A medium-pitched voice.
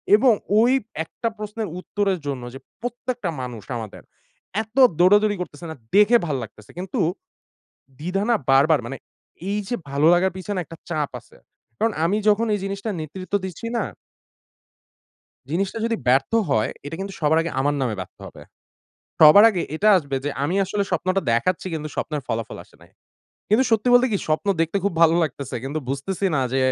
Yes: medium, 180 Hz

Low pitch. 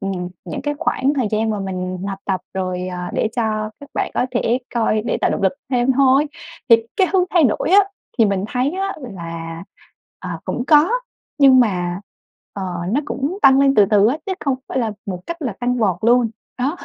No: high, 230 Hz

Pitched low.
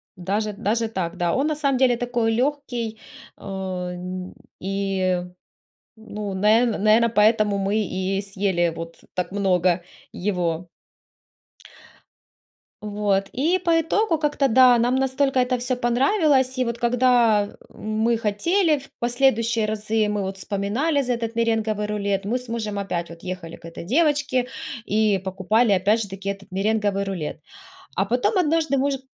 No: high, 215 Hz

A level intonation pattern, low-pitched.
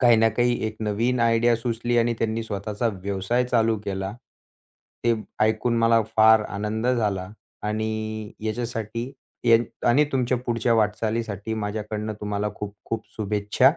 Yes: narrow, 1.8 semitones; low, 110 Hz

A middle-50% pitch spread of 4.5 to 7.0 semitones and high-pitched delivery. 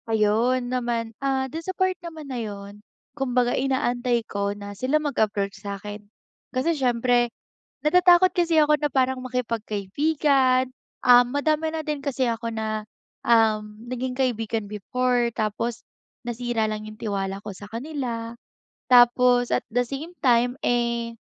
No: average, 3.4 semitones; high, 245 Hz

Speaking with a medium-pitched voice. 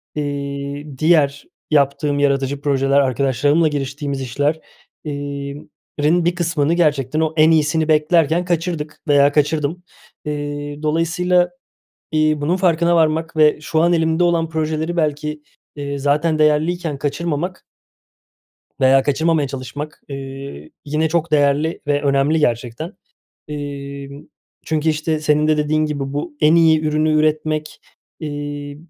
Yes: medium, 150 Hz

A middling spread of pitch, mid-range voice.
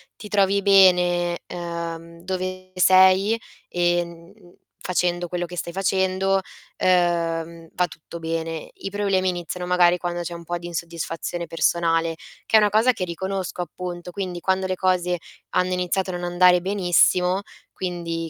No: narrow, 1.6 semitones; medium, 180 Hz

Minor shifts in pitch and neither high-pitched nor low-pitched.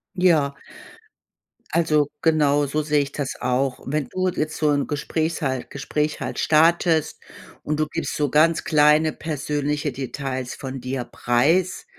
Yes: narrow, 2.2 semitones; medium, 150 Hz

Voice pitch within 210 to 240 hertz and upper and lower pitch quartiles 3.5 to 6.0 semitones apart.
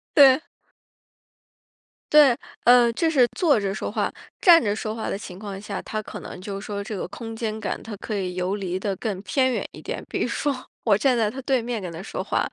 Yes: high, 215 Hz; average, 3.9 semitones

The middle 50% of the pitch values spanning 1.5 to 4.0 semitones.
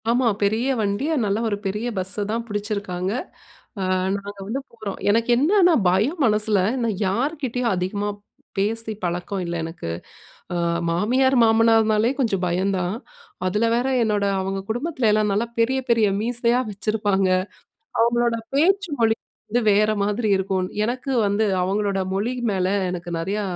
Yes: average, 3.2 semitones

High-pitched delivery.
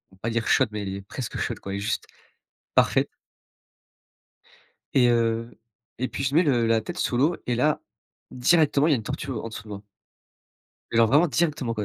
No: low, 120 Hz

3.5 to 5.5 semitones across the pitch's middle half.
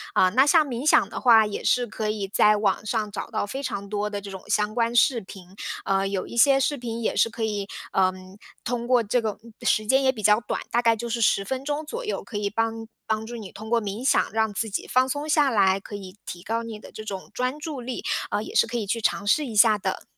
No: average, 3.0 semitones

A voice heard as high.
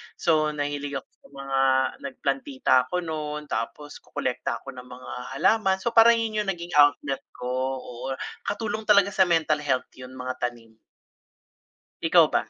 No: medium, 145 Hz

